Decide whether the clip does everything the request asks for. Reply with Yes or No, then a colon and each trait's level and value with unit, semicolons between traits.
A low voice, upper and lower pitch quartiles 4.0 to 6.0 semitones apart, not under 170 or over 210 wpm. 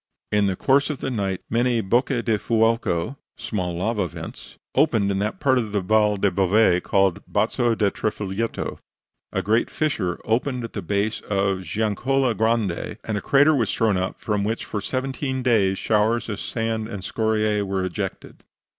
No: low, 110 Hz; average, 3.2 semitones; average, 180 wpm